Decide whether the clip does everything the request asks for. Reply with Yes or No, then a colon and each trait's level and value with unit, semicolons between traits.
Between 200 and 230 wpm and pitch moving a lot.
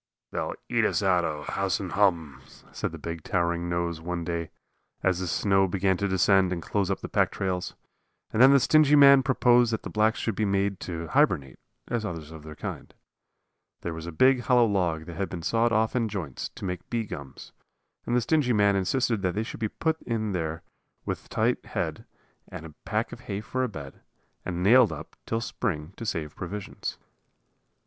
No: fast, 205 wpm; average, 4.9 semitones